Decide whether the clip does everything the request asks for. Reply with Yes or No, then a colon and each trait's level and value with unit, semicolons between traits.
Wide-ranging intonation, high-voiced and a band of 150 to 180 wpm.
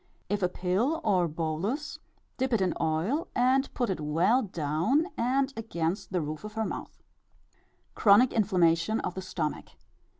Yes: wide, 6.5 semitones; high, 195 Hz; average, 155 wpm